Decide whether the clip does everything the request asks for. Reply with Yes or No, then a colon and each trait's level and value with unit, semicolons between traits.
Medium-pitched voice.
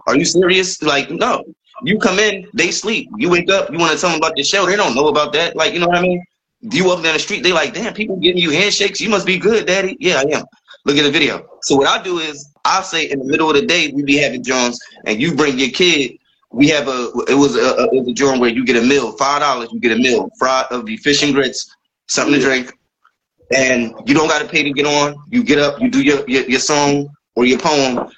Yes: medium, 150 Hz